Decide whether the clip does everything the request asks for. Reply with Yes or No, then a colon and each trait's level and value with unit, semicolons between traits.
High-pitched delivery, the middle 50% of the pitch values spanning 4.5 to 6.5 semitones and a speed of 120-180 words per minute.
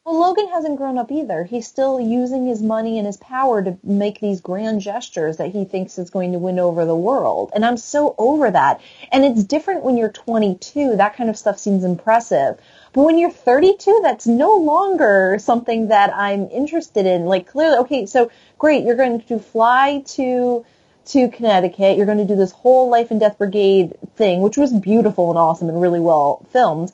No: high, 225 Hz; average, 5.1 semitones; average, 200 wpm